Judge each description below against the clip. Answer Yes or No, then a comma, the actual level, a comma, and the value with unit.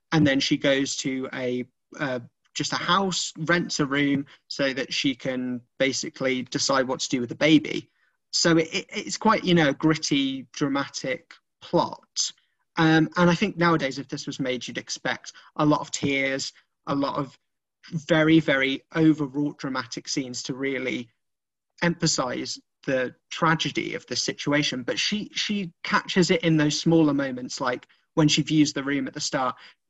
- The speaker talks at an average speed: Yes, average, 170 wpm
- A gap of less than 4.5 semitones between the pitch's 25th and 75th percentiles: Yes, average, 3.4 semitones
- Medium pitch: Yes, medium, 145 Hz